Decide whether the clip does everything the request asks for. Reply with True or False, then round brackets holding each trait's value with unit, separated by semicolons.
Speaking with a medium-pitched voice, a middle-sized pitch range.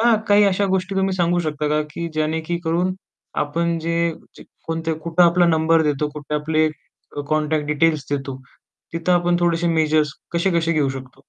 False (165 Hz; 2.2 semitones)